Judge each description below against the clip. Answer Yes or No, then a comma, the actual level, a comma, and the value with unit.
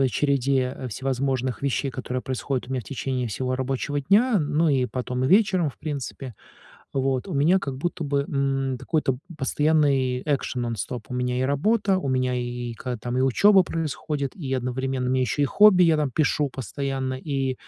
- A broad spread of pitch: No, narrow, 2.6 semitones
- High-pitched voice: No, low, 135 Hz